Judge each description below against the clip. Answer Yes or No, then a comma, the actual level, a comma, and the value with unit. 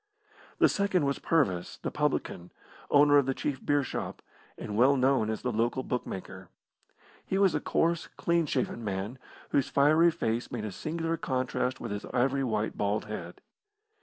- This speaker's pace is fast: No, average, 165 wpm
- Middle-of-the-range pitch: No, low, 130 Hz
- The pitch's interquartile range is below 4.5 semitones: No, average, 5.1 semitones